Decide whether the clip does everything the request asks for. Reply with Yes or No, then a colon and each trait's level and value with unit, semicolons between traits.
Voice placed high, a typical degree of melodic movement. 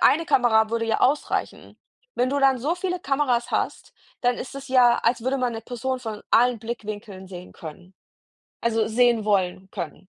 Yes: high, 235 Hz; average, 3.3 semitones